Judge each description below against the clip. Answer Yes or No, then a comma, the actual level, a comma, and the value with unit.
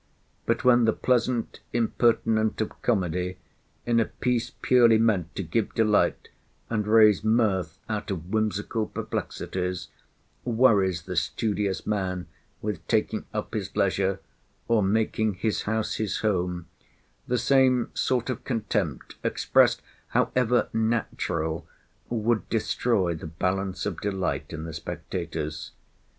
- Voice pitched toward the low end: Yes, low, 105 Hz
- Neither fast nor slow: No, slow, 125 wpm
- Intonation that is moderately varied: Yes, average, 3.9 semitones